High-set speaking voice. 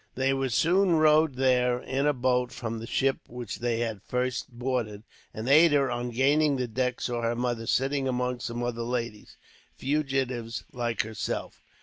No: low, 125 Hz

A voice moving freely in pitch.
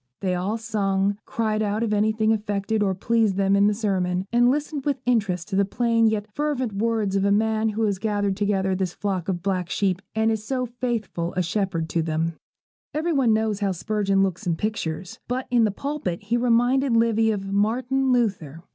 No: average, 3.0 semitones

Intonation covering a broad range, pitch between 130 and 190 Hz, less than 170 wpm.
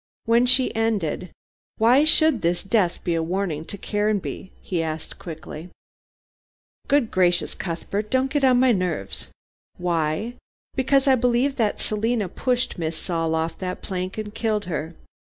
No: wide, 6.0 semitones; high, 200 Hz; average, 150 wpm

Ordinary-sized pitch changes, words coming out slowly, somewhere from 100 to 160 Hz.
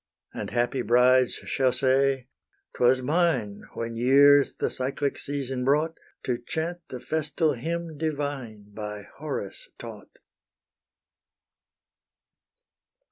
Yes: average, 3.5 semitones; slow, 100 wpm; low, 135 Hz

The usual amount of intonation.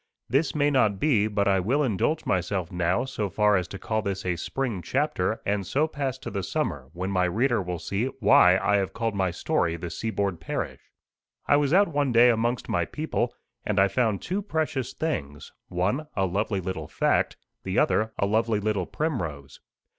No: wide, 6.0 semitones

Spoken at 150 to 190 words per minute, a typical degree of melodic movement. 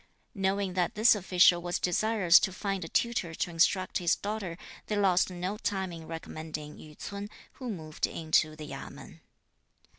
Yes: average, 160 wpm; average, 3.5 semitones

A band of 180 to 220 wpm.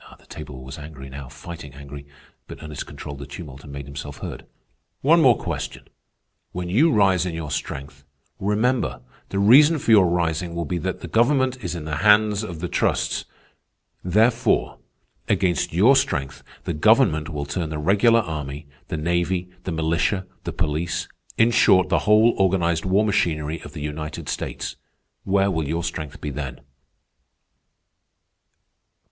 No: average, 155 wpm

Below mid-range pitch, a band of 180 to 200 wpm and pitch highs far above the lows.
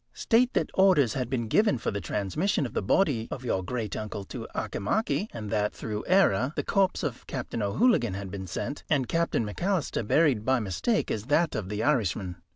Yes: low, 120 Hz; average, 195 wpm; wide, 8.1 semitones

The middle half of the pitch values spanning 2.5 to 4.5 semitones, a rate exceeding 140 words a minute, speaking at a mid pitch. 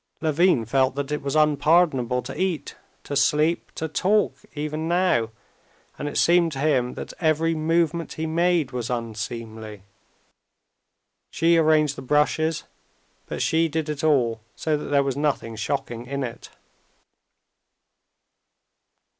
No: average, 4.1 semitones; slow, 135 wpm; medium, 150 Hz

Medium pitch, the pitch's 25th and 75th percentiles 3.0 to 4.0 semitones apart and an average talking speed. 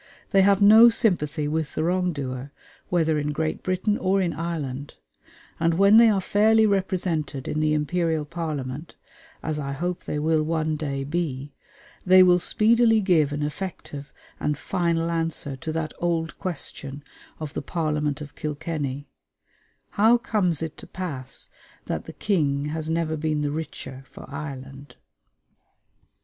Yes: medium, 160 Hz; average, 3.5 semitones; average, 150 wpm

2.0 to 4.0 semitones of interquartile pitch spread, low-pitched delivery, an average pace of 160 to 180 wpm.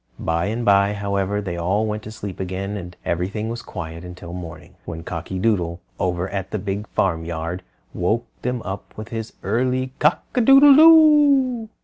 No: average, 4.6 semitones; low, 100 Hz; average, 170 wpm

